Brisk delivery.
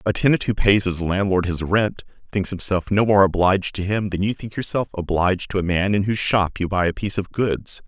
Yes: fast, 245 wpm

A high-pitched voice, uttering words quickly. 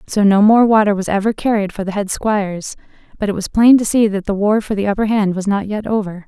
Yes: high, 205 Hz; fast, 260 wpm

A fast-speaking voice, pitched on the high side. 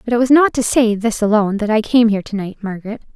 Yes: fast, 285 wpm; high, 220 Hz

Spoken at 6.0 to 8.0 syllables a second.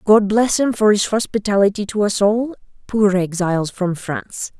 No: 4.8 syllables/s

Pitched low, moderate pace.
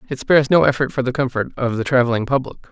No: low, 130 Hz; fast, 245 wpm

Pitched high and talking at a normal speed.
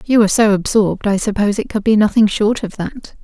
No: high, 210 Hz; fast, 240 wpm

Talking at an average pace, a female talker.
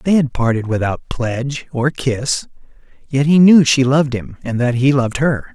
No: average, 195 wpm; male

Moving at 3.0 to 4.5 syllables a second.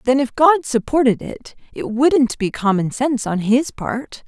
Yes: 4.3 syllables/s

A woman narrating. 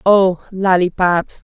Yes: female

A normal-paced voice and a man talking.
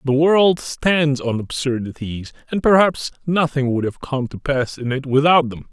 Yes: average, 180 wpm; male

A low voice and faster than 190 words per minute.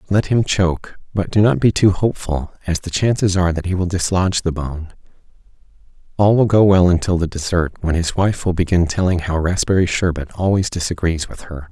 Yes: very low, 90 Hz; average, 200 wpm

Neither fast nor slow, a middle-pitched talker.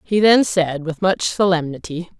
Yes: average, 165 wpm; medium, 175 Hz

